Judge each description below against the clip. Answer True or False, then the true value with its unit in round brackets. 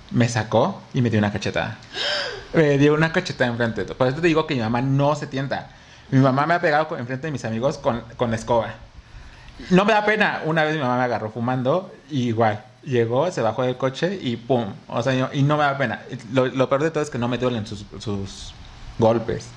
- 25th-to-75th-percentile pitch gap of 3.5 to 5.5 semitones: True (4.0 semitones)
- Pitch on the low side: True (125 Hz)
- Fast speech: True (240 wpm)